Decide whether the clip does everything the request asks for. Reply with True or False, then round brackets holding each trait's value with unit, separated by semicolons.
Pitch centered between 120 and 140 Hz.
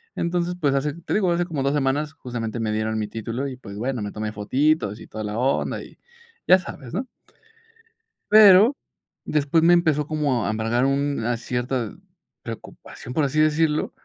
True (135 Hz)